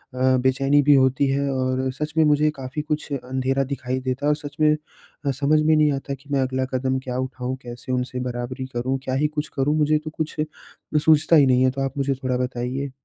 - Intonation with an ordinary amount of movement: No, narrow, 2.2 semitones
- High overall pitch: No, low, 135 Hz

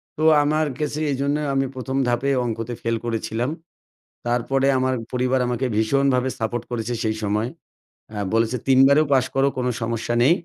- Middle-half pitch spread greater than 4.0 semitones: No, average, 2.7 semitones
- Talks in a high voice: No, low, 125 Hz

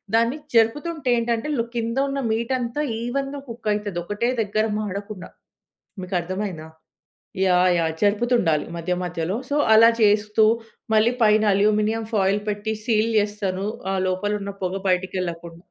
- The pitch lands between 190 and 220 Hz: Yes, high, 210 Hz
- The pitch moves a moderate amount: Yes, average, 3.5 semitones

